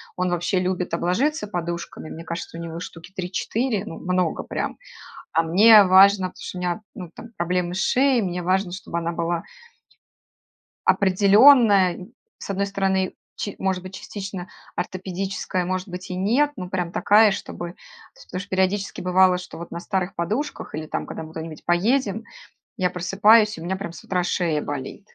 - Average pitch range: No, narrow, 2.3 semitones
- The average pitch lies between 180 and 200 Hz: Yes, medium, 185 Hz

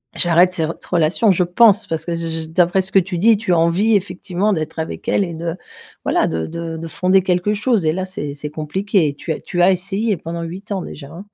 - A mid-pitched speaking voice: Yes, medium, 175 Hz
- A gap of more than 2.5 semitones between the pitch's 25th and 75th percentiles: Yes, average, 2.9 semitones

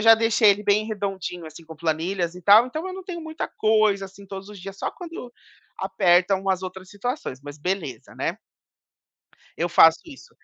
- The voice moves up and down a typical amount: Yes, average, 3.7 semitones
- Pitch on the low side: No, high, 195 Hz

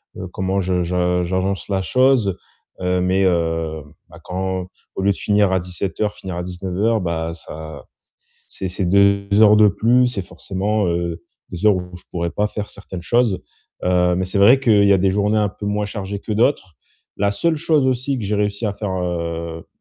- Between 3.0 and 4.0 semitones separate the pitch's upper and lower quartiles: No, narrow, 2.6 semitones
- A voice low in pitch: Yes, very low, 95 Hz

